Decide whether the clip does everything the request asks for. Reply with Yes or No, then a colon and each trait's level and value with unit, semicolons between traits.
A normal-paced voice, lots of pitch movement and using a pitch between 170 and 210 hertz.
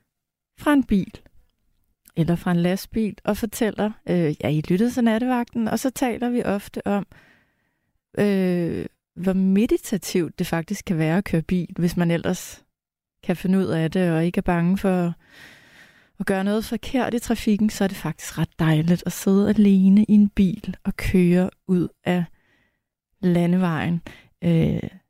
No: average, 165 wpm; average, 3.3 semitones; high, 190 Hz